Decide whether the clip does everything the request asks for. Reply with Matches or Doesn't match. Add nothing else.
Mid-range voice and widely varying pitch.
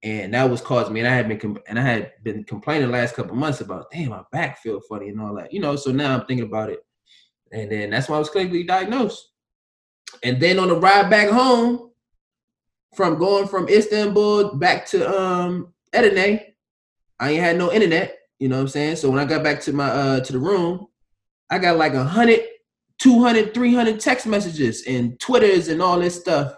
Matches